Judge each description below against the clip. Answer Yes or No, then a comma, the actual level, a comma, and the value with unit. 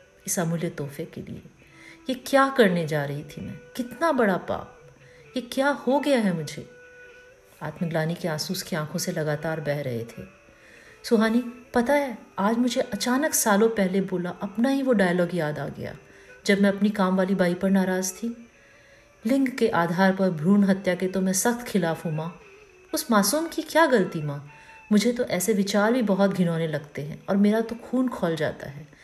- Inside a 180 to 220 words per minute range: Yes, average, 185 wpm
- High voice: Yes, high, 195 Hz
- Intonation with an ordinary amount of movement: No, wide, 6.3 semitones